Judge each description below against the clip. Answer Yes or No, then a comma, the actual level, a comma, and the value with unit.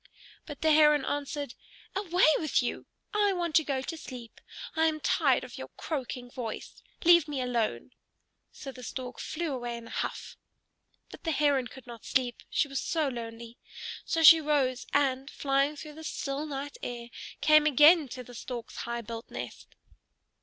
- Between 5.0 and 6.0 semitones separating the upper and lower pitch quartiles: No, average, 3.8 semitones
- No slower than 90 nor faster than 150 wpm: No, average, 175 wpm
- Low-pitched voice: No, very high, 275 Hz